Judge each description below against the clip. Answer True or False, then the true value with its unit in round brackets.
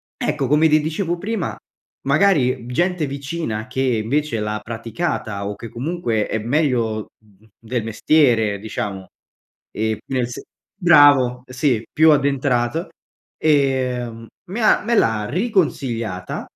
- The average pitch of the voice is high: False (130 Hz)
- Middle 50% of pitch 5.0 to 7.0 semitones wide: True (5.4 semitones)